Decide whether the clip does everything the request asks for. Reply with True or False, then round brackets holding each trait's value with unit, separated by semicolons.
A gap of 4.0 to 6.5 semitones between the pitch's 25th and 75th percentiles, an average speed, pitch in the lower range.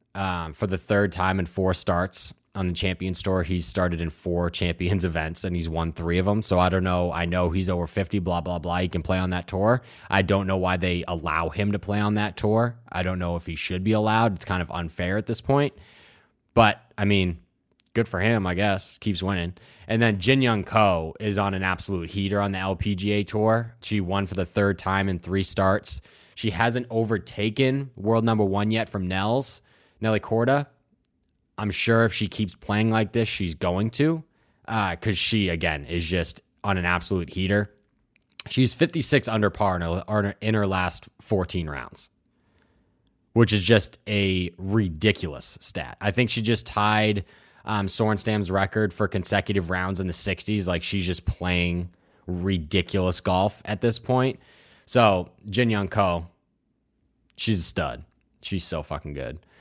False (3.2 semitones; 185 wpm; 100 Hz)